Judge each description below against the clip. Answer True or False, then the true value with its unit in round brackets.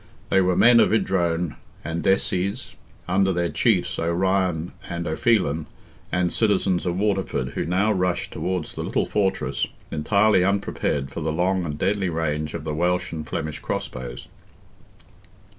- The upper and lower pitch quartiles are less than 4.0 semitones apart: True (3.0 semitones)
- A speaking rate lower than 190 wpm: True (145 wpm)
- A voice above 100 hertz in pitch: False (90 Hz)